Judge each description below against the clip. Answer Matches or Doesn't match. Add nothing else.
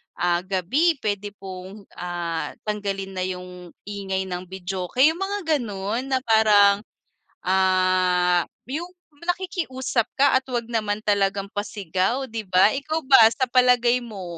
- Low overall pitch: Doesn't match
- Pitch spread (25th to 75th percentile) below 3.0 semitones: Doesn't match